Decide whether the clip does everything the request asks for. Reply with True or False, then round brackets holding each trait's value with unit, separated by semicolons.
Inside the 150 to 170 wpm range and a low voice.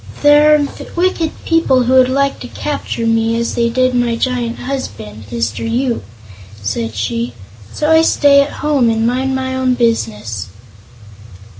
False (155 wpm; 245 Hz)